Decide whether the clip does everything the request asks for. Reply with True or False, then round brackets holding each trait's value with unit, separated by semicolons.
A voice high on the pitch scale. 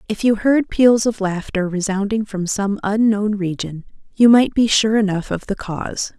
True (210 Hz)